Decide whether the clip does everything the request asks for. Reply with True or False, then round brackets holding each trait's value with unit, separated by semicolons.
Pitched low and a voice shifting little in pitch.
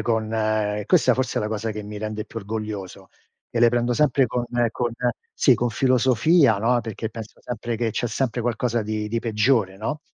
True (115 Hz; 2.3 semitones)